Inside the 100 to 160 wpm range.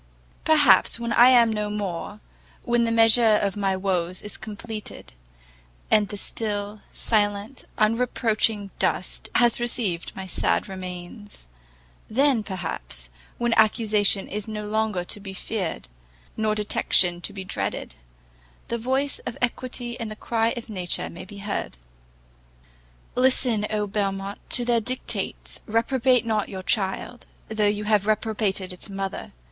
Yes: average, 140 wpm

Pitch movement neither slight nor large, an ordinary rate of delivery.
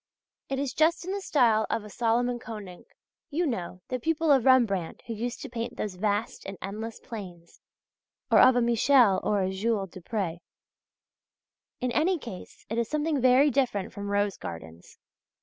Yes: average, 4.7 semitones; average, 170 wpm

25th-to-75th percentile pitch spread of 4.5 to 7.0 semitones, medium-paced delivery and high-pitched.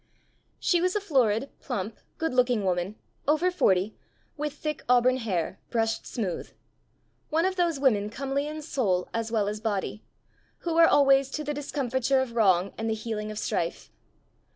Yes: wide, 5.6 semitones; average, 165 wpm; high, 245 Hz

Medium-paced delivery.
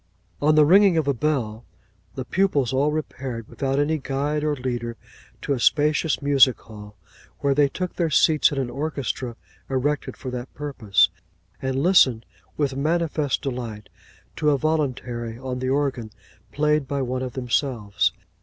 Yes: average, 155 wpm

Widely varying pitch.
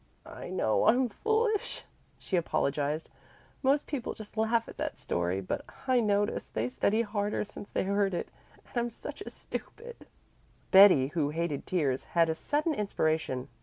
Yes: wide, 7.4 semitones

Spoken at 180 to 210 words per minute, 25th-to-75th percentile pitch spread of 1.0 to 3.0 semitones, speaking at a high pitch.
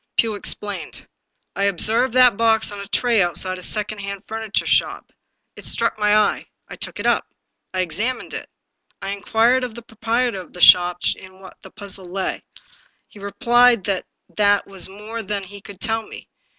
Yes: average, 190 wpm; average, 2.7 semitones; high, 205 Hz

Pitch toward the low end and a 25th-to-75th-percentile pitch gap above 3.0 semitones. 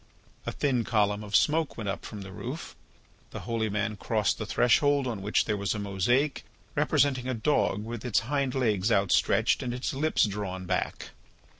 Yes: low, 110 Hz; average, 3.9 semitones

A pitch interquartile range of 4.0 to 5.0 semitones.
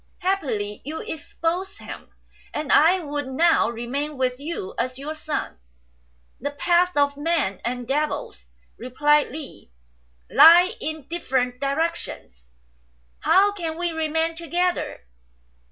Yes: average, 4.3 semitones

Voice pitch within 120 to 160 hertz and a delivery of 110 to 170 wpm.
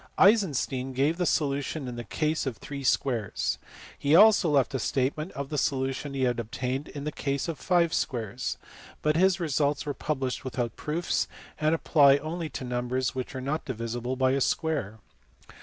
No: medium, 140 Hz; average, 180 wpm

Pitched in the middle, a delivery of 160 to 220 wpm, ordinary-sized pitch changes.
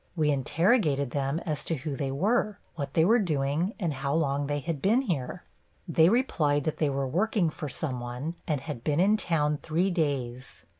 Yes: medium, 150 Hz; average, 195 wpm; average, 4.0 semitones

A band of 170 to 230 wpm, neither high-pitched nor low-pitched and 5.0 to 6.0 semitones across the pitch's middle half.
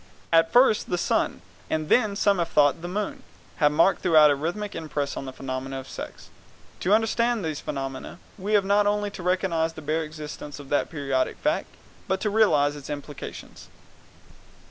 Yes: average, 185 wpm; medium, 165 Hz; wide, 5.6 semitones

